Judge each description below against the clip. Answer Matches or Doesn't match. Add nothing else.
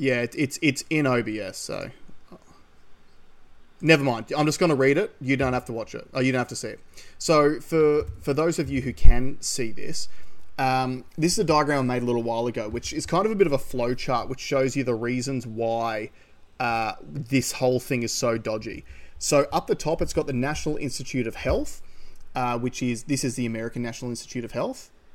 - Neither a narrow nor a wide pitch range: Matches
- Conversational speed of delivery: Doesn't match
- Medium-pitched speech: Doesn't match